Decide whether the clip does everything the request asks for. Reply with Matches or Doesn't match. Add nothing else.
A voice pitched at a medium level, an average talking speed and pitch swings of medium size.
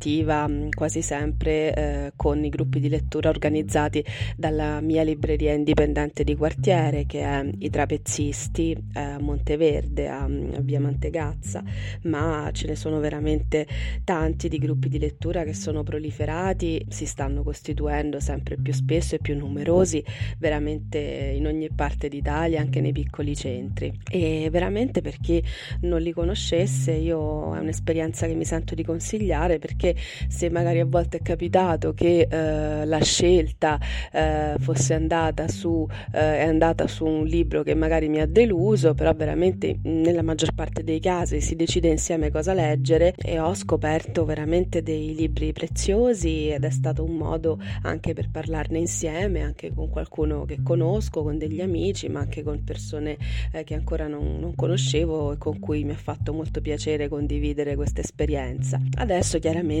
Doesn't match